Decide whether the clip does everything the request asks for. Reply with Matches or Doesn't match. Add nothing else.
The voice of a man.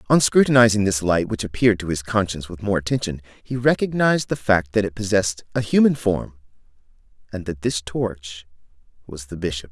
Matches